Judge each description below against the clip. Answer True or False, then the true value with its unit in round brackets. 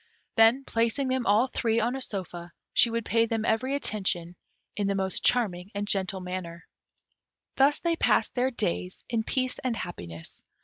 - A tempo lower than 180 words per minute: True (170 wpm)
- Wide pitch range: False (5.0 semitones)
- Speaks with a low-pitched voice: False (220 Hz)